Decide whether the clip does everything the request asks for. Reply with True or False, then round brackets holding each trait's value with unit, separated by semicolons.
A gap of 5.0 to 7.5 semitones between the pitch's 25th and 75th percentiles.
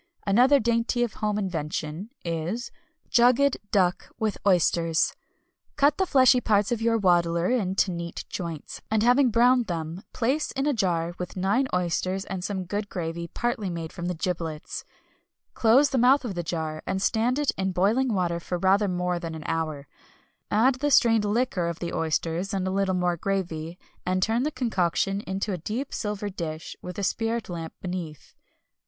True (5.3 semitones)